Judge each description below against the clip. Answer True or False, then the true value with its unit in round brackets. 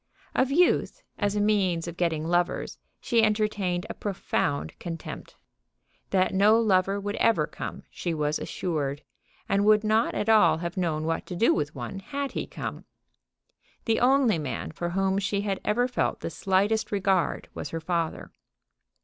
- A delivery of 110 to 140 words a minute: False (165 wpm)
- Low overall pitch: False (195 Hz)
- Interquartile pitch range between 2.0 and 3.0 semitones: False (4.0 semitones)